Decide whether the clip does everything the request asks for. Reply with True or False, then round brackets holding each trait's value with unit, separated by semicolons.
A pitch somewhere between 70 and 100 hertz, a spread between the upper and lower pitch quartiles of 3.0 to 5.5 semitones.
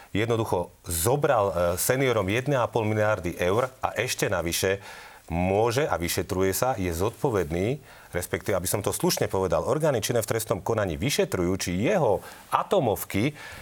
True (95 Hz; 3.4 semitones)